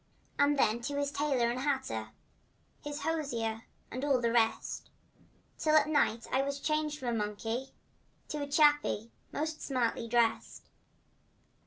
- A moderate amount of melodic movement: Yes, average, 4.1 semitones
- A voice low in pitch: No, very high, 270 Hz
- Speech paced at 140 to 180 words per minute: Yes, average, 150 wpm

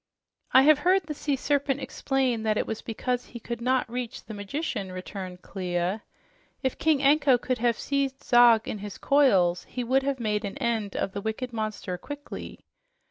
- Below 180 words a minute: No, average, 185 wpm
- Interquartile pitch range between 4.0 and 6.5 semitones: Yes, average, 4.5 semitones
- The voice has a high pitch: Yes, high, 240 Hz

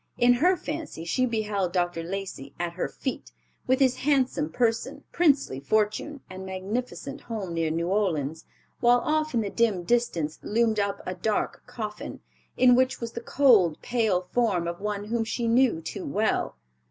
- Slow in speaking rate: No, average, 165 wpm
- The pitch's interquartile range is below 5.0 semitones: No, wide, 5.4 semitones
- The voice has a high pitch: Yes, high, 215 Hz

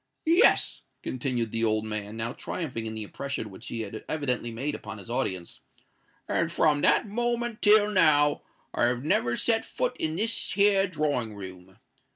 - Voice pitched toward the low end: Yes, low, 130 Hz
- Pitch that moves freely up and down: Yes, wide, 8.7 semitones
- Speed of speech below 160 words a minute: No, average, 165 wpm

